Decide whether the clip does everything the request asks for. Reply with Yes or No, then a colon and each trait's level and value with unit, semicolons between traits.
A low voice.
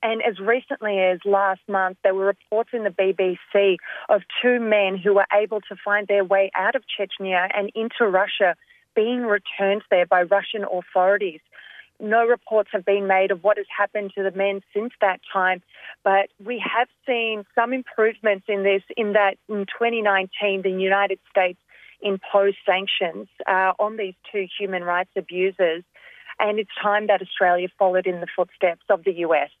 No: high, 200 Hz